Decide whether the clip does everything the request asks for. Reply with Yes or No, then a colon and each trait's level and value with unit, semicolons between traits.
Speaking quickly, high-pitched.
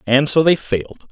No: fast, 215 wpm; medium, 140 Hz